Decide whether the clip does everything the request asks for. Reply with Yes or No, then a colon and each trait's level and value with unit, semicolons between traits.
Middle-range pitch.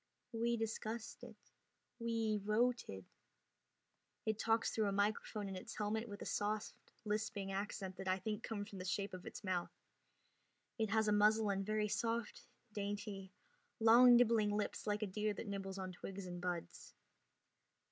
No: high, 210 Hz